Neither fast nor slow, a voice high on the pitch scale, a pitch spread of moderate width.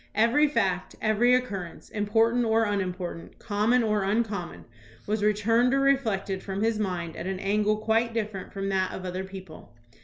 Yes: average, 160 wpm; high, 210 Hz; average, 3.0 semitones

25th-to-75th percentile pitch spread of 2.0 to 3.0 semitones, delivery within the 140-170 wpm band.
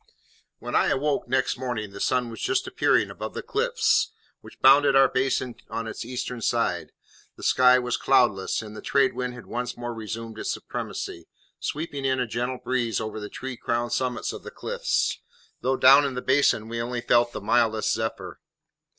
No: narrow, 2.5 semitones; average, 185 wpm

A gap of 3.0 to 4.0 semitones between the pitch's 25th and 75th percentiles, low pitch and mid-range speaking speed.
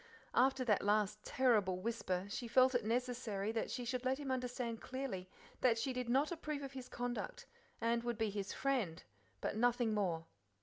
No: average, 3.4 semitones; high, 240 Hz; average, 180 wpm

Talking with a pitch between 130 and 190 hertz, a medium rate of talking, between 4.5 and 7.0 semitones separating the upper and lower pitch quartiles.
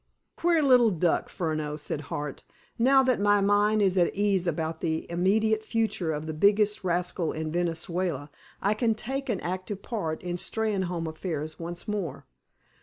Yes: medium, 185 Hz; average, 160 wpm; average, 4.8 semitones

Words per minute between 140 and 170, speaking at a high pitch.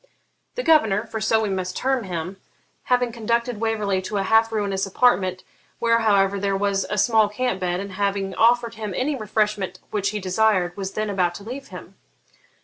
No: average, 185 wpm; high, 210 Hz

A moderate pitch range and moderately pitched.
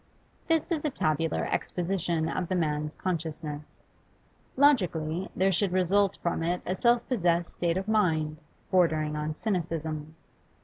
Yes: average, 3.5 semitones; medium, 170 Hz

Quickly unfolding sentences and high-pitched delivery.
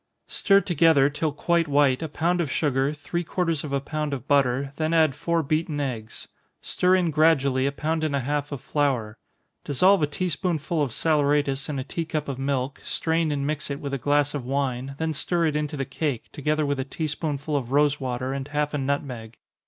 No: fast, 215 wpm; medium, 145 Hz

